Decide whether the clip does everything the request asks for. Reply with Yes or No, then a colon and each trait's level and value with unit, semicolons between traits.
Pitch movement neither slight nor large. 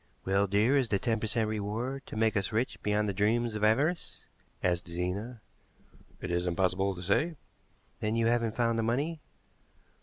Yes: average, 3.2 semitones